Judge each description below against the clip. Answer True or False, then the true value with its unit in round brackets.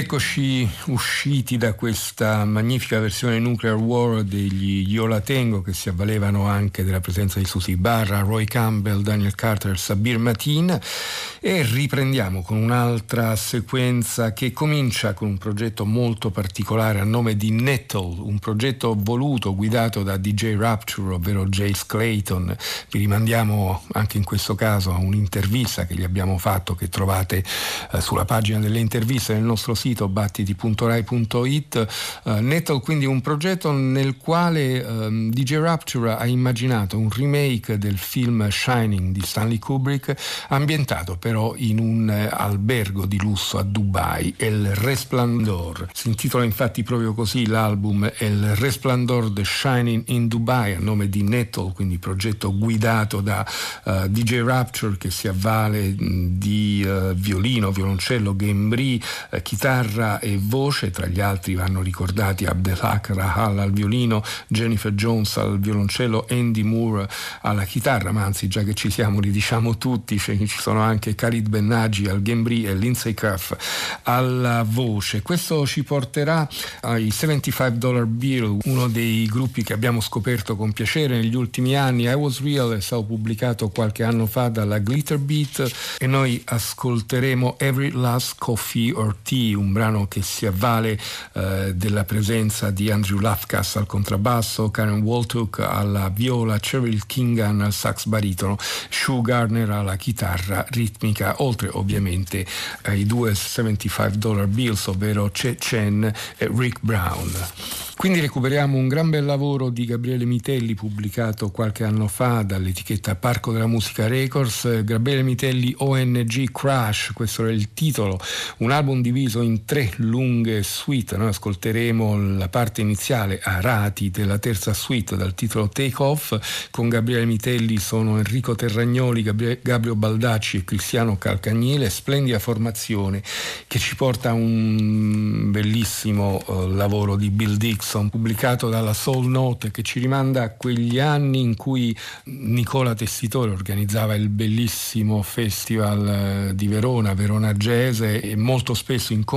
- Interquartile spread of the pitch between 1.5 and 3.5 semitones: True (3.0 semitones)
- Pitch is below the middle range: True (110 Hz)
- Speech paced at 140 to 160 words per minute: True (145 wpm)